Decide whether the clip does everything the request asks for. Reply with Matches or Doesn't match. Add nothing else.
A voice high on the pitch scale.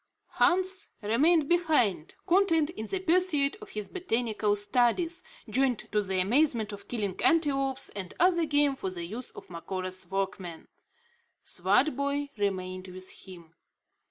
Matches